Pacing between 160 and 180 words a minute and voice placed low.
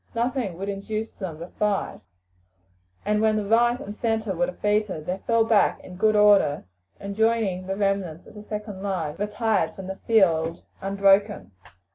No: average, 165 wpm; high, 205 Hz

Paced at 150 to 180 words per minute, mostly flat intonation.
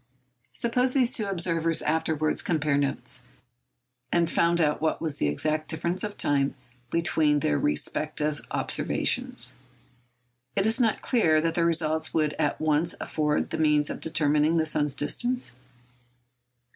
No: average, 140 wpm; narrow, 2.3 semitones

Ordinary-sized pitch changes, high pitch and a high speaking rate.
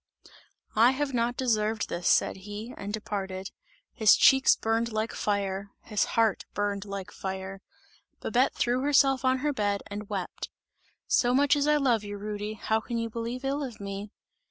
No: average, 3.7 semitones; high, 220 Hz; average, 170 wpm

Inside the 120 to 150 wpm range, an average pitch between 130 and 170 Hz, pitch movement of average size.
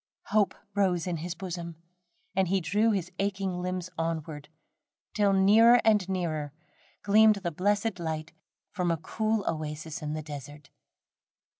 No: average, 140 wpm; medium, 180 Hz; average, 4.0 semitones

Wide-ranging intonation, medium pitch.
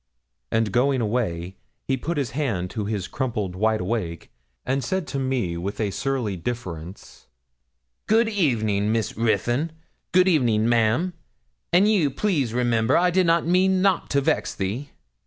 No: wide, 6.8 semitones; low, 120 Hz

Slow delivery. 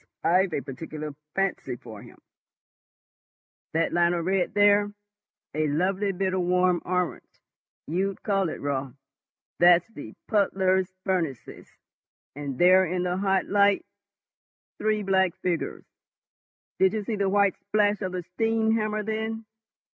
Yes: slow, 125 wpm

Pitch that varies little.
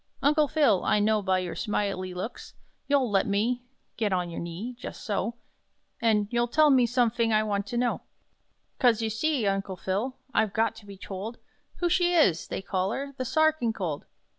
No: average, 4.2 semitones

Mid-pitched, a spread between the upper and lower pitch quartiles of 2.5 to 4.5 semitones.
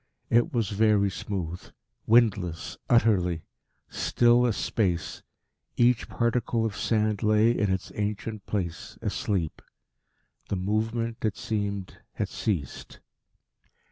No: low, 105 Hz; average, 3.1 semitones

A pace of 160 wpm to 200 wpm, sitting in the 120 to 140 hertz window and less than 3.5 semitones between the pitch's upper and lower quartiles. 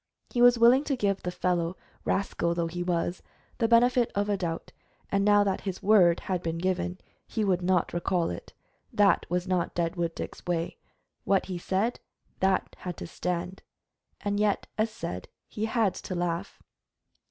No: average, 175 wpm; medium, 185 Hz; average, 2.9 semitones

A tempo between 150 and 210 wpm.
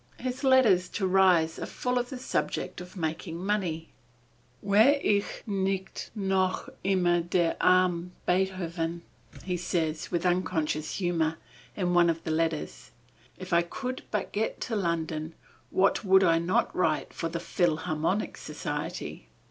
No: average, 140 wpm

